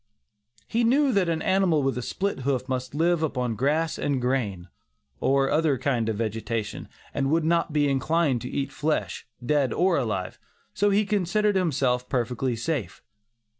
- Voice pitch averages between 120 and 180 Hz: Yes, medium, 140 Hz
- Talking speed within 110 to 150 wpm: No, average, 165 wpm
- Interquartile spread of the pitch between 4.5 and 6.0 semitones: Yes, average, 5.2 semitones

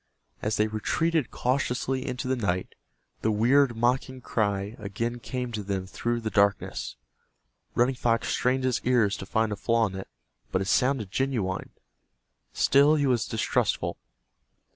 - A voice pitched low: Yes, low, 115 Hz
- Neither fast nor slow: Yes, average, 150 wpm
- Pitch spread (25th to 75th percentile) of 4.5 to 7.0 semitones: No, average, 3.7 semitones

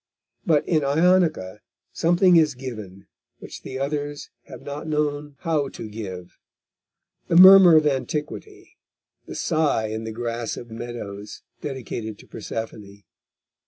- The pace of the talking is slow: Yes, slow, 125 wpm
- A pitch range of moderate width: No, wide, 5.8 semitones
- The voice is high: No, medium, 140 Hz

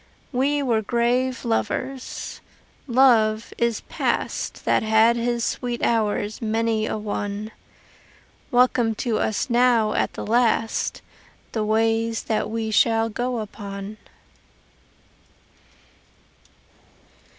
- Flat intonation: Yes, narrow, 2.0 semitones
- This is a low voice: No, high, 225 Hz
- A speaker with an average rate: No, slow, 100 wpm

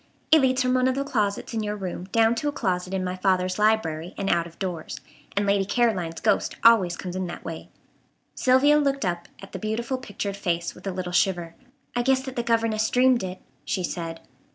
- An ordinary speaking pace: No, fast, 215 wpm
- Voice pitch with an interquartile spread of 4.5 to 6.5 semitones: Yes, average, 4.9 semitones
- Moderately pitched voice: No, high, 200 Hz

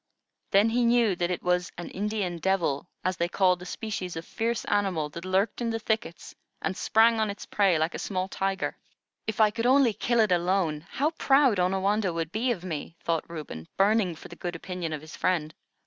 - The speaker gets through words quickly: Yes, fast, 210 wpm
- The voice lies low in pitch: No, high, 190 Hz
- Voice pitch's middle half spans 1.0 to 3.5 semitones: No, average, 4.1 semitones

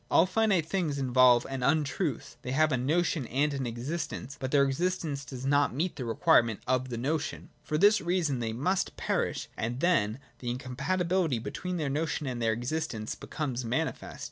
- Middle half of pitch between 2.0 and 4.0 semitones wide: No, average, 4.7 semitones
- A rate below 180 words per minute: Yes, average, 170 wpm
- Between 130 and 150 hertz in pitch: Yes, medium, 140 Hz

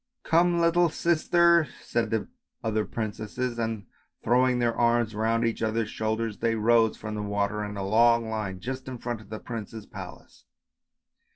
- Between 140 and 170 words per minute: No, average, 180 wpm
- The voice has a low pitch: Yes, low, 115 Hz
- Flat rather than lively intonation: Yes, narrow, 2.2 semitones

